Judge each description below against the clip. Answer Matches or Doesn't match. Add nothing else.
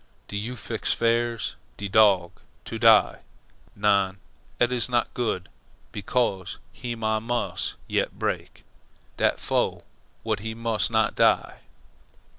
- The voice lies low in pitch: Matches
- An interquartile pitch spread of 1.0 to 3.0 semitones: Matches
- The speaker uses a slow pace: Matches